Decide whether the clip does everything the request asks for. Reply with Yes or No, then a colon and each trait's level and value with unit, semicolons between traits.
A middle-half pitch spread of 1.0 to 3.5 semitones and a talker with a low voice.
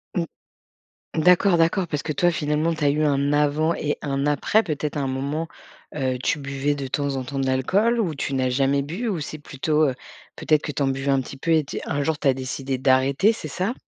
No: average, 2.8 semitones; medium, 145 Hz